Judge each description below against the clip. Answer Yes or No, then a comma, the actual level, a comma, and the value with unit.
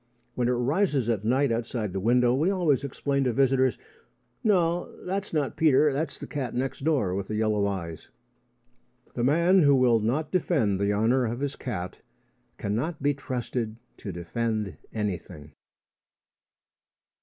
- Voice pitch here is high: No, low, 125 Hz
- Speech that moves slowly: No, average, 150 wpm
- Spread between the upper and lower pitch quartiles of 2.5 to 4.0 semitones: No, average, 5.0 semitones